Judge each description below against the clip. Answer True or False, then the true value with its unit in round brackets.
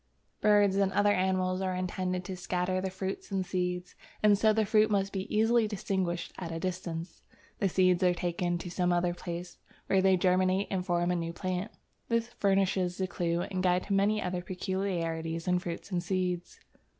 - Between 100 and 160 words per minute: False (185 wpm)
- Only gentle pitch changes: True (1.6 semitones)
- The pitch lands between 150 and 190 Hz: True (185 Hz)